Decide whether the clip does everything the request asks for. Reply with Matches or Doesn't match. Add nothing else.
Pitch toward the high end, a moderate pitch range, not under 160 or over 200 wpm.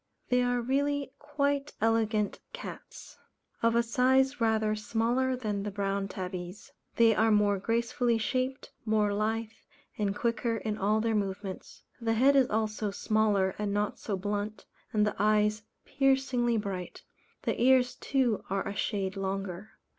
Doesn't match